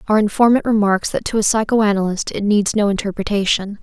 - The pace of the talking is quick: No, average, 175 wpm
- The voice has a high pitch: Yes, high, 205 Hz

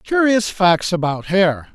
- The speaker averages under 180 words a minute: Yes, average, 140 wpm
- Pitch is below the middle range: No, high, 190 Hz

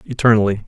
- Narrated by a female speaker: No, male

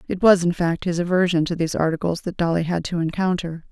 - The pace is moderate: No, fast, 225 wpm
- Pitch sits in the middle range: Yes, medium, 170 Hz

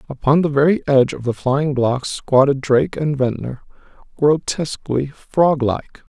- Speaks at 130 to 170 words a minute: Yes, average, 145 wpm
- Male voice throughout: Yes, male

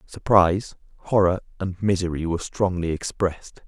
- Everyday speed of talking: No, slow, 115 wpm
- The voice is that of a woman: No, male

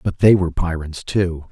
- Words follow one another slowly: No, average, 200 wpm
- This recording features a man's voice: Yes, male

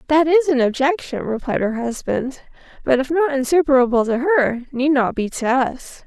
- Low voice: No, very high, 270 Hz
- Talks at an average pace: Yes, average, 180 wpm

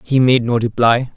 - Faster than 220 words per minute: No, fast, 205 wpm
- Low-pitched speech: Yes, low, 120 Hz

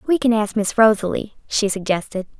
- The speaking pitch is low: No, high, 215 Hz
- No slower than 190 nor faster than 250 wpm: No, average, 175 wpm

